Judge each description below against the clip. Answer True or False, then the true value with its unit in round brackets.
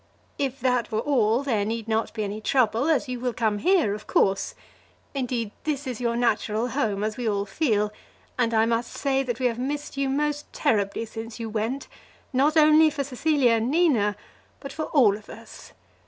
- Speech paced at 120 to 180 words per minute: False (195 wpm)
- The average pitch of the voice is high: True (240 Hz)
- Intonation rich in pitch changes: False (4.1 semitones)